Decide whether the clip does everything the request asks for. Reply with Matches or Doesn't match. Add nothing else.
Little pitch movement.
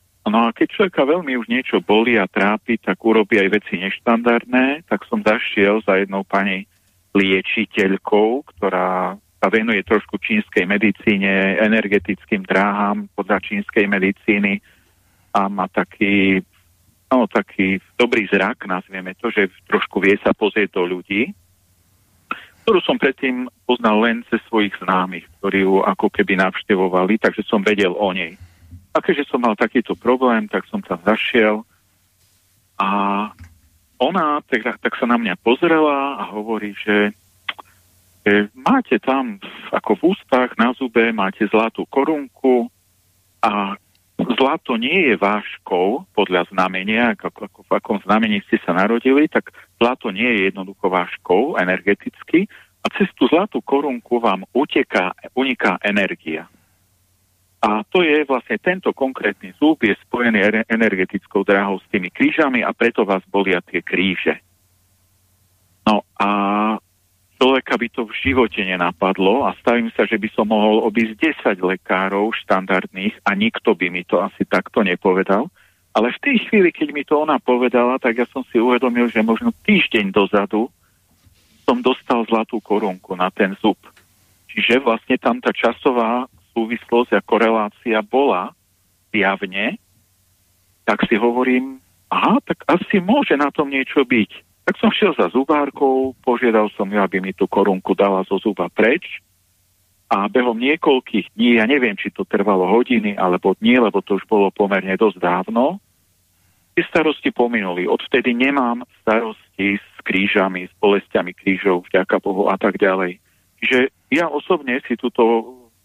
Doesn't match